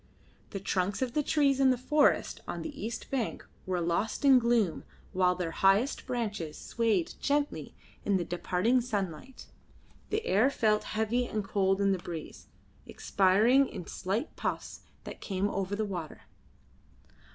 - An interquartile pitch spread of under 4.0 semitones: No, average, 5.0 semitones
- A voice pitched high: Yes, high, 210 Hz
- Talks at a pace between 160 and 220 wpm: No, average, 150 wpm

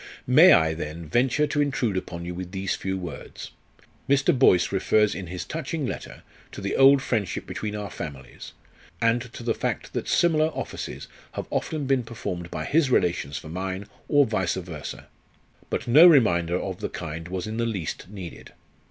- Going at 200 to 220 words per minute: No, average, 180 wpm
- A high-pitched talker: No, low, 100 Hz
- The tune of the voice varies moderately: No, wide, 6.8 semitones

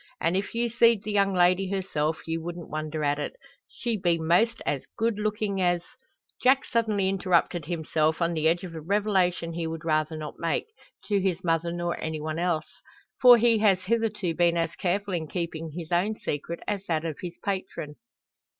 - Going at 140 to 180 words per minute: No, average, 195 wpm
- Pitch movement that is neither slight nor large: Yes, average, 3.6 semitones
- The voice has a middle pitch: Yes, medium, 175 Hz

